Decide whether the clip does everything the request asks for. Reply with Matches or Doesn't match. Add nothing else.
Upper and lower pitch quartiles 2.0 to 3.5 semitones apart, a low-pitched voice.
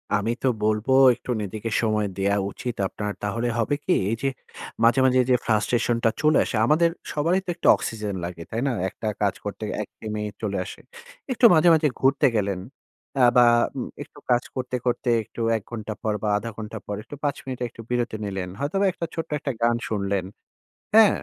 Doesn't match